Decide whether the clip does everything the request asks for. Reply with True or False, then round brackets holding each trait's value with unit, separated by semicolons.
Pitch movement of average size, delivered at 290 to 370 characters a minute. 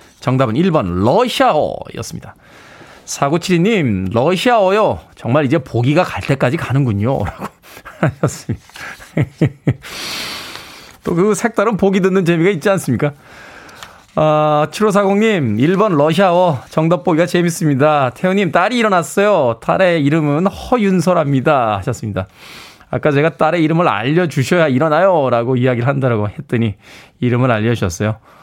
False (6.4 semitones; 300 characters per minute)